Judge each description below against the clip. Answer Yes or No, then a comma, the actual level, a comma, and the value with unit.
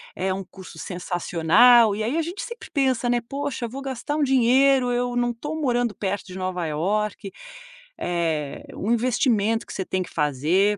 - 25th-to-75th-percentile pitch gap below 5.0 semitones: No, wide, 5.4 semitones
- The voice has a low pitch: No, high, 225 Hz